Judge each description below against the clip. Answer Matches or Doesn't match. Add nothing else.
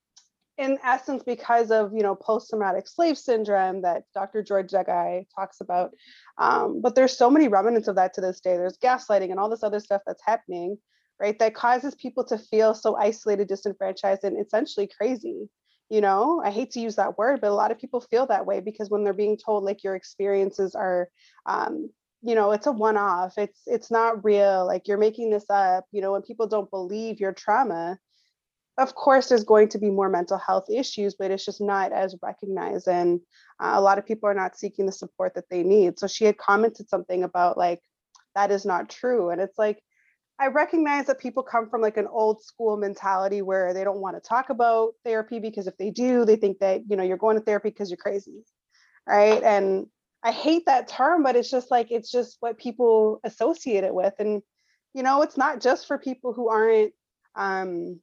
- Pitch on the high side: Matches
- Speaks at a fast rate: Matches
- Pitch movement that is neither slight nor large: Matches